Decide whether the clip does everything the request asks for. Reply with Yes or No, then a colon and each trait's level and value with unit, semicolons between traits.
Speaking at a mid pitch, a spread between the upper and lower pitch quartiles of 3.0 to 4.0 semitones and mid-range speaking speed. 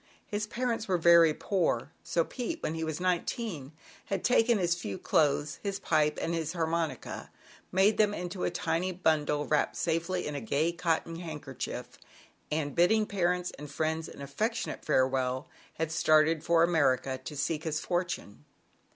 Yes: medium, 165 Hz; average, 3.3 semitones; average, 170 wpm